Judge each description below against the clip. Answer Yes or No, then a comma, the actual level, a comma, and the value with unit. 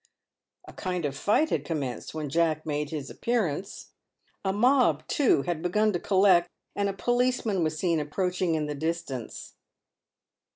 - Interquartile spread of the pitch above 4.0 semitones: Yes, average, 4.7 semitones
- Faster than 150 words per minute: Yes, average, 160 wpm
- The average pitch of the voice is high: No, medium, 175 Hz